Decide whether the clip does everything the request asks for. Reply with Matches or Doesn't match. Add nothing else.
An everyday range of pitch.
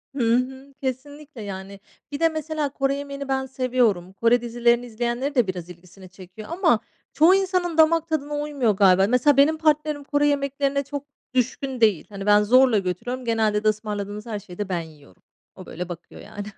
Doesn't match